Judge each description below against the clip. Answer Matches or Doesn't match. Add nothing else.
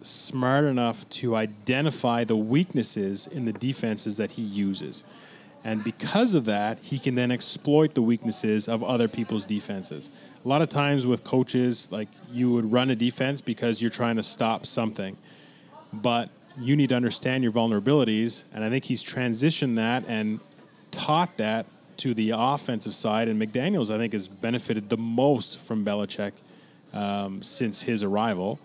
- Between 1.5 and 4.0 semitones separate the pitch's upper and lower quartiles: Matches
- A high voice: Doesn't match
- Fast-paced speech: Doesn't match